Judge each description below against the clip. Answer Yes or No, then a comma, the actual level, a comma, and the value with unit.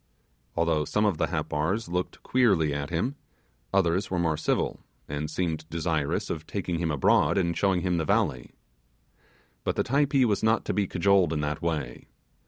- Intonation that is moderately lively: Yes, average, 4.2 semitones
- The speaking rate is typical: Yes, average, 175 wpm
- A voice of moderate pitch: No, very low, 85 Hz